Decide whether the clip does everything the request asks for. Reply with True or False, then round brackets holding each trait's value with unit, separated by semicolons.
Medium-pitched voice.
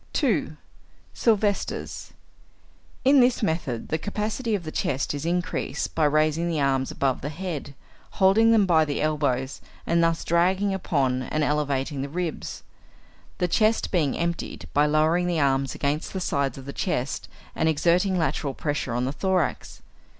True (160 Hz)